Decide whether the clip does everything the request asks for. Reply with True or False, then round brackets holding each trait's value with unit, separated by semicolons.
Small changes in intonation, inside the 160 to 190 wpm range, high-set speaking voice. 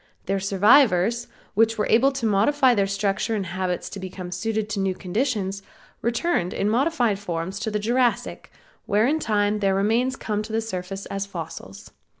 False (3.1 semitones; 170 wpm; 205 Hz)